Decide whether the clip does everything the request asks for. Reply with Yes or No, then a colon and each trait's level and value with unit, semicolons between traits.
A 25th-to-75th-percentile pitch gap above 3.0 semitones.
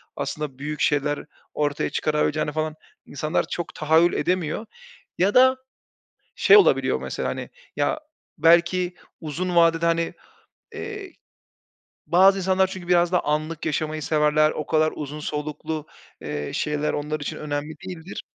No: average, 2.7 semitones